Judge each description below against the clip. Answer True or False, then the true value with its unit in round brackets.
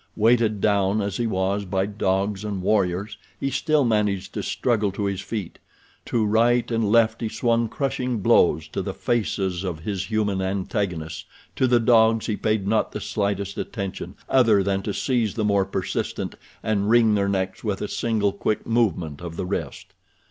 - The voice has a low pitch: True (105 Hz)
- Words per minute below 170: False (175 wpm)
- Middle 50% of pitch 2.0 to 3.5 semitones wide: True (2.7 semitones)